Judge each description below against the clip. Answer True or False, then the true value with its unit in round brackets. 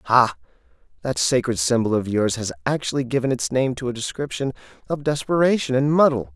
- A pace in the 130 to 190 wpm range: True (170 wpm)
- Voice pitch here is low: True (125 Hz)